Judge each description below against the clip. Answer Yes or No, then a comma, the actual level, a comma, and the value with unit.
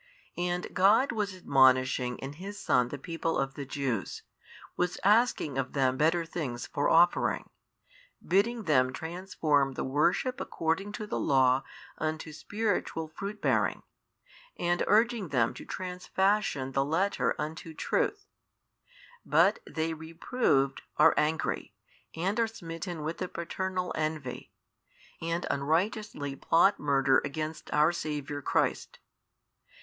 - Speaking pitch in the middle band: Yes, medium, 160 Hz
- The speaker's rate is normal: No, slow, 125 wpm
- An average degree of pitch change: Yes, average, 5.0 semitones